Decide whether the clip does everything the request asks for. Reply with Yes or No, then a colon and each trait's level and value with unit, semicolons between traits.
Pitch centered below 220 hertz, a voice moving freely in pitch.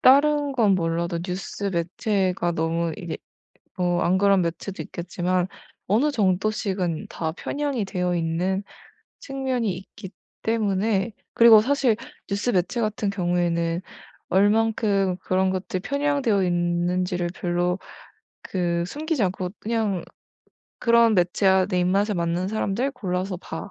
No: high, 190 Hz; average, 3.7 semitones